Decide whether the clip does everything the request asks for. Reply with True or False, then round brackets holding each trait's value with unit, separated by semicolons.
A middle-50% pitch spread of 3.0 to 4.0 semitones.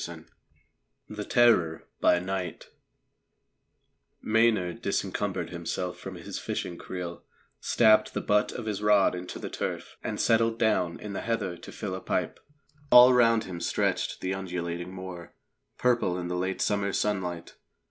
True (3.6 semitones)